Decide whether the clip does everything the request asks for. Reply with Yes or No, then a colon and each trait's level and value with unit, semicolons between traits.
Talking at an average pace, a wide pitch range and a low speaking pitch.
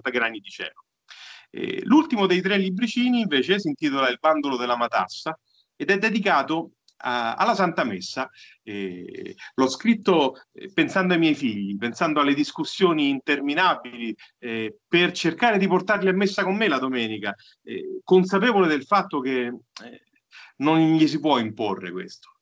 No: average, 150 wpm; wide, 7.5 semitones; medium, 165 Hz